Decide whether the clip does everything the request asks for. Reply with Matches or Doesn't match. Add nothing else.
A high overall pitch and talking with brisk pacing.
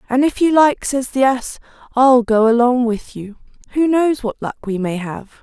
Matches